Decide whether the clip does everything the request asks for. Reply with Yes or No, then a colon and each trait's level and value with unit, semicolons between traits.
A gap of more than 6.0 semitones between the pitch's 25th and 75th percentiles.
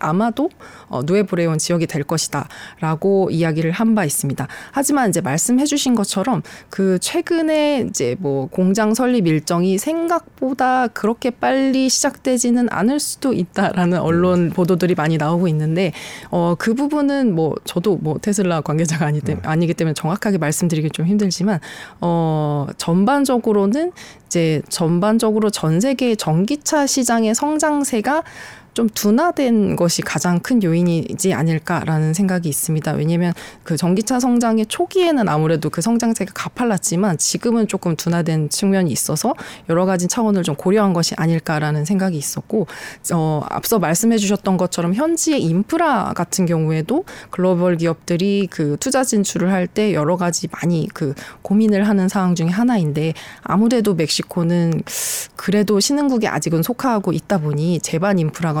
No: wide, 5.6 semitones